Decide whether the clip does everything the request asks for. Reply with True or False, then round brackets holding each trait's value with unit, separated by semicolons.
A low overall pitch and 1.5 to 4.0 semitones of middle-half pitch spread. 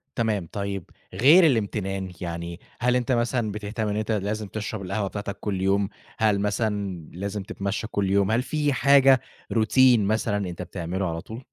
True (105 Hz; 2.8 semitones)